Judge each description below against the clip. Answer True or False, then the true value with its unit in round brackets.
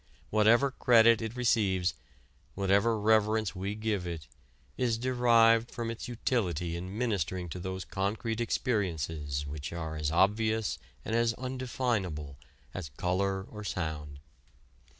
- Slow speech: True (125 wpm)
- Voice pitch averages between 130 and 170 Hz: False (105 Hz)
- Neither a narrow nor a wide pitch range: True (4.7 semitones)